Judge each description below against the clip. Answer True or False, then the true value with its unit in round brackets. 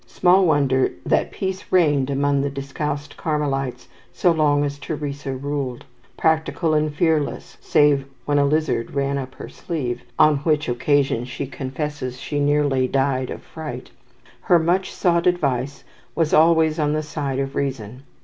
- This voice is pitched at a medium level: True (145 Hz)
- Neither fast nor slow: True (155 wpm)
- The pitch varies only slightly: True (2.3 semitones)